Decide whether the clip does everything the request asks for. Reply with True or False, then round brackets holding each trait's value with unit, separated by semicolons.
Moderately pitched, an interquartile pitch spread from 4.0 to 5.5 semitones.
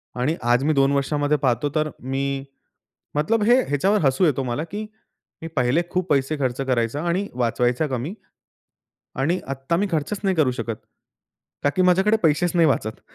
True (145 Hz; 4.6 semitones)